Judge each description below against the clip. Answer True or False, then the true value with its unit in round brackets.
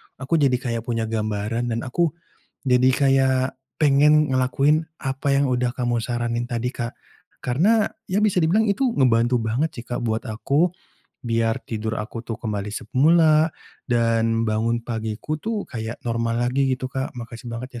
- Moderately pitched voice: False (125 Hz)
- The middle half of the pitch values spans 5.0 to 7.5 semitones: False (3.3 semitones)